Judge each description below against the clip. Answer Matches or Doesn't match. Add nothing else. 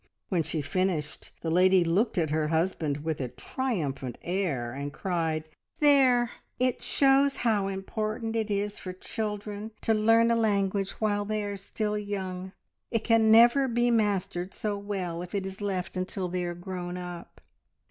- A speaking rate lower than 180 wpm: Matches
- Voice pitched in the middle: Doesn't match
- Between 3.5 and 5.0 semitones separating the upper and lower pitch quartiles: Matches